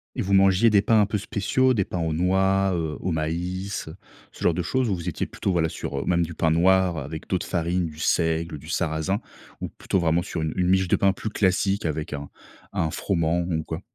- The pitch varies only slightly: No, average, 3.1 semitones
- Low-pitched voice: Yes, very low, 90 Hz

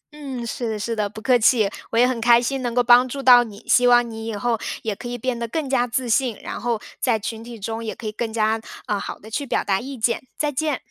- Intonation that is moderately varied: No, narrow, 2.0 semitones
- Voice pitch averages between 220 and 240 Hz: Yes, high, 235 Hz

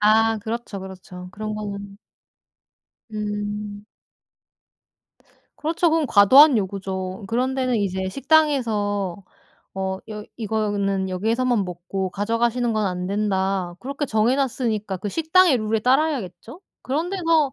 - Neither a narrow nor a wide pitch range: Yes, average, 4.5 semitones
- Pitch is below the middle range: No, high, 215 Hz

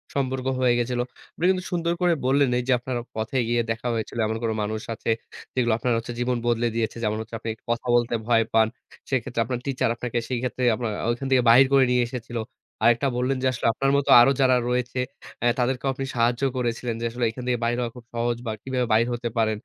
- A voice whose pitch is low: Yes, low, 120 Hz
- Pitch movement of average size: No, narrow, 1.7 semitones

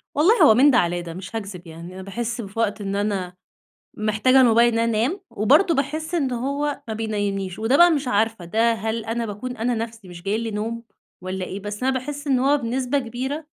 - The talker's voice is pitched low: No, high, 230 Hz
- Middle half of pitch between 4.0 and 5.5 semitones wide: Yes, average, 4.3 semitones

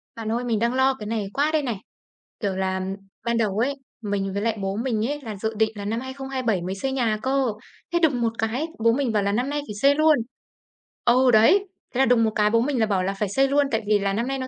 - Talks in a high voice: Yes, high, 230 Hz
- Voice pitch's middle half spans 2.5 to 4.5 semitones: Yes, average, 4.1 semitones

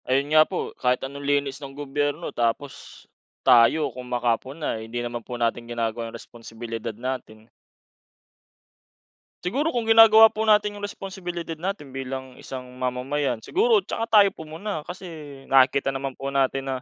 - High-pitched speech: No, low, 135 Hz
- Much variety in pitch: Yes, wide, 6.1 semitones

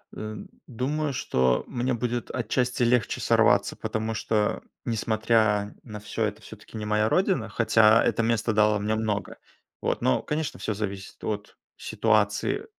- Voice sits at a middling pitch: No, low, 110 Hz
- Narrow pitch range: Yes, narrow, 2.2 semitones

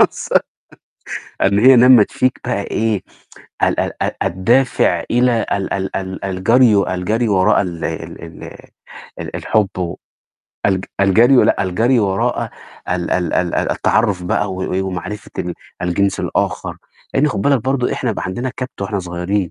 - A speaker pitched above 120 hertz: No, low, 100 Hz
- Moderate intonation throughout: Yes, average, 4.4 semitones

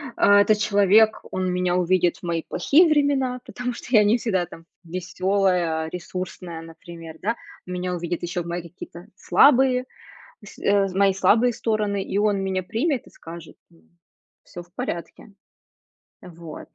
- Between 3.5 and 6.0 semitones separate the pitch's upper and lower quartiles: Yes, average, 3.8 semitones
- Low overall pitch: No, medium, 185 Hz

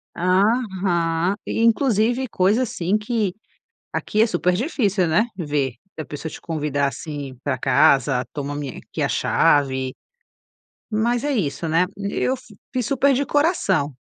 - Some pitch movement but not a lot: No, wide, 7.5 semitones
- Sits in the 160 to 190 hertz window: Yes, medium, 185 Hz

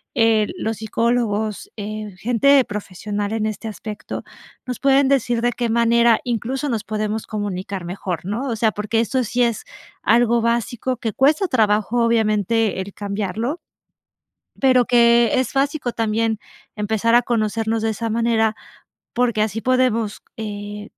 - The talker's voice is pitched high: Yes, high, 225 Hz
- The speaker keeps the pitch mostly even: Yes, narrow, 2.2 semitones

